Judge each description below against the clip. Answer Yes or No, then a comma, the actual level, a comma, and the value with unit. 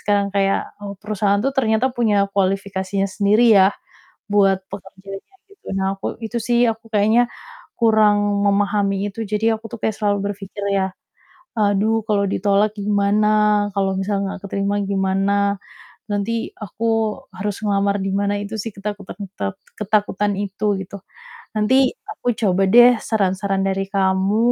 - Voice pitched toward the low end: No, high, 200 Hz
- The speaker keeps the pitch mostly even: Yes, narrow, 1.4 semitones